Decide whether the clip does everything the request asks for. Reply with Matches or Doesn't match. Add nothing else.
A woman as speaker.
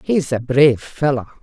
Matches